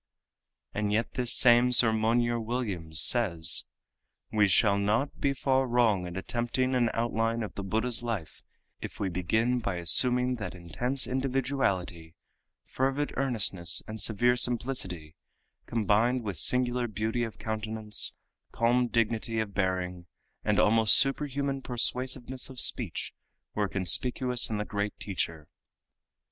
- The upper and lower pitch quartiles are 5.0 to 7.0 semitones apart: No, average, 3.8 semitones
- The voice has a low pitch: Yes, low, 115 Hz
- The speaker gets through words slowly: Yes, slow, 130 wpm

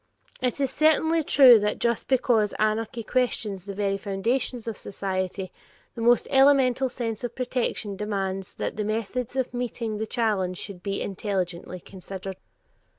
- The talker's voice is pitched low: No, high, 220 Hz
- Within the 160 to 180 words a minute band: No, average, 150 wpm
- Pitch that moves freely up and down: No, average, 4.0 semitones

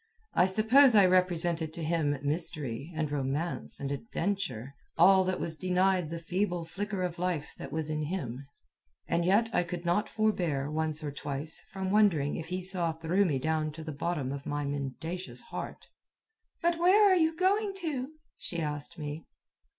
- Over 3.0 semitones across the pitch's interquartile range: Yes, average, 4.2 semitones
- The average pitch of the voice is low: No, medium, 170 Hz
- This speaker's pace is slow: No, average, 175 wpm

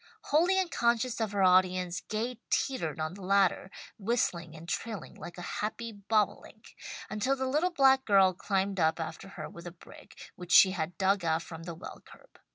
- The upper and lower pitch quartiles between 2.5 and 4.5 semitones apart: No, average, 5.0 semitones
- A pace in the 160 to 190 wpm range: Yes, average, 180 wpm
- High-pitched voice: Yes, high, 195 Hz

